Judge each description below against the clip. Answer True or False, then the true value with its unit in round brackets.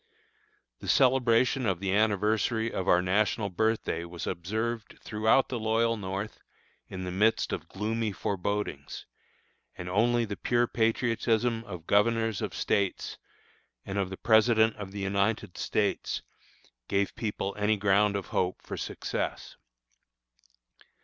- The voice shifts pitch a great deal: False (2.6 semitones)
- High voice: False (105 Hz)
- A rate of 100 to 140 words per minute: True (135 wpm)